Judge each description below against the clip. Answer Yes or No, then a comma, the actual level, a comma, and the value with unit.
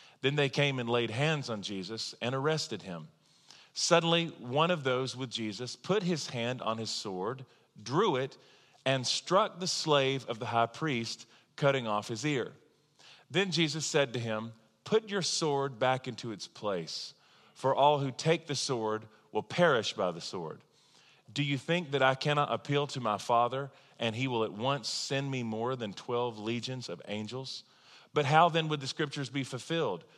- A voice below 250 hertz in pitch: Yes, low, 135 Hz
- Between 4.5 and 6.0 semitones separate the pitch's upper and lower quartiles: No, average, 4.1 semitones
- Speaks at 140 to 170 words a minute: No, average, 180 wpm